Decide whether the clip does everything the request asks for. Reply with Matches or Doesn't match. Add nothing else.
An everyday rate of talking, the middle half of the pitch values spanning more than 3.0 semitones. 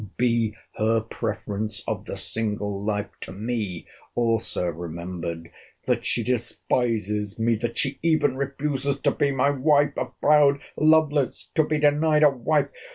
Doesn't match